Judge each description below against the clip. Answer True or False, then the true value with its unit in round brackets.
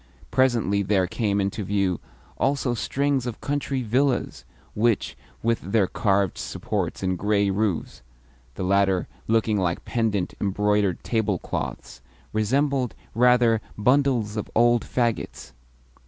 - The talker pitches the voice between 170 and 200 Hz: False (110 Hz)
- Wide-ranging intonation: False (3.6 semitones)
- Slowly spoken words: True (115 wpm)